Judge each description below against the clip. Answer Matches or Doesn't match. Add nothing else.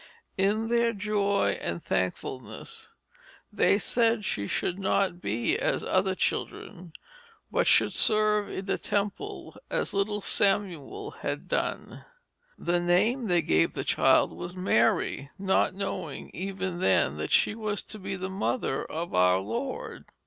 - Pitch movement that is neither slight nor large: Matches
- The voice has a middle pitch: Doesn't match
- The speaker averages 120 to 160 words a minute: Matches